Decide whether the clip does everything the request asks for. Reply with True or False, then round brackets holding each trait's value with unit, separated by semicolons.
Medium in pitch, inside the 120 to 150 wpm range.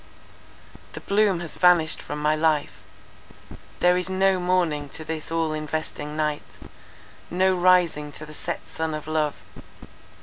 True (160 Hz; 135 wpm)